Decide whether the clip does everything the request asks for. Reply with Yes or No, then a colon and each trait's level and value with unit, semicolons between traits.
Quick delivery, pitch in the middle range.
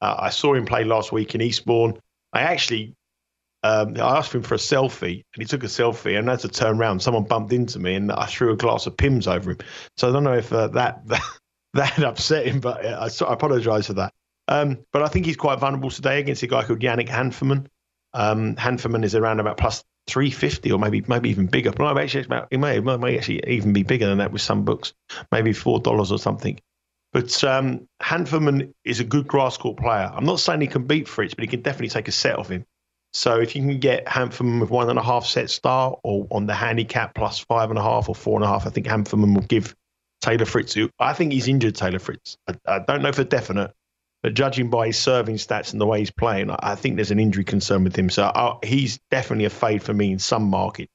No: fast, 245 wpm; low, 115 Hz